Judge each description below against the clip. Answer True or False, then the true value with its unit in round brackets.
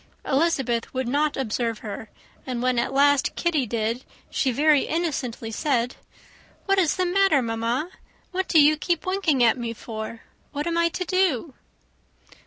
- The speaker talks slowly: False (160 wpm)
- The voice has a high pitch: True (275 Hz)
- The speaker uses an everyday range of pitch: False (6.0 semitones)